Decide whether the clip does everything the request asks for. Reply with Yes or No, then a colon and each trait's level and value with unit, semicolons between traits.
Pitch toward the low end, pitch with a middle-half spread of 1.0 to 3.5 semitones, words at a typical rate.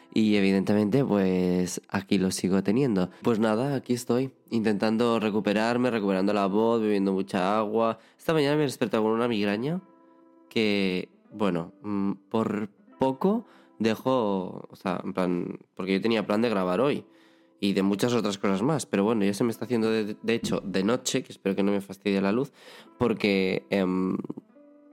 Yes: low, 105 Hz; average, 3.0 semitones; average, 170 wpm